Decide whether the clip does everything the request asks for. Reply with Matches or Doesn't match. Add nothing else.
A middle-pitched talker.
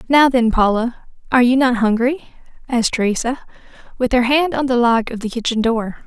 Doesn't match